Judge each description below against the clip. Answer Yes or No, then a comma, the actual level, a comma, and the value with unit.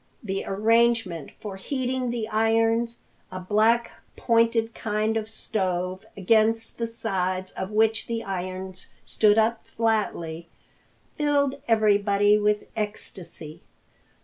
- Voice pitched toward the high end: Yes, high, 215 Hz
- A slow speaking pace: Yes, slow, 110 wpm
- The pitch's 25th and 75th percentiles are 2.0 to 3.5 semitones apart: Yes, average, 3.0 semitones